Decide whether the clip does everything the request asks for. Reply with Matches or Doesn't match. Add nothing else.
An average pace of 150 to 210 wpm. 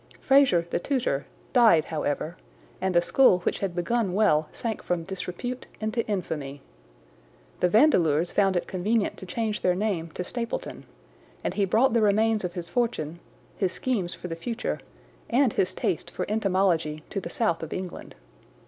Matches